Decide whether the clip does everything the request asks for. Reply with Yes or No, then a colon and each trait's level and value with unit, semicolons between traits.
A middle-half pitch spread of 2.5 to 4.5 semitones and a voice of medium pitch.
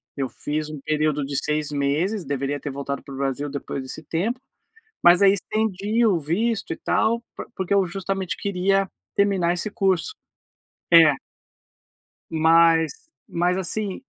No: average, 4.9 semitones; medium, 170 Hz